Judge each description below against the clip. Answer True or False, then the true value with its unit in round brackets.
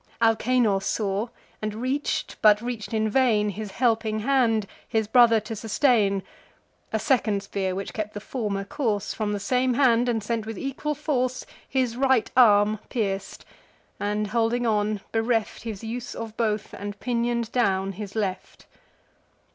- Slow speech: False (150 wpm)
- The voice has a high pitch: True (220 Hz)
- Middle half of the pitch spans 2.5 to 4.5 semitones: True (2.8 semitones)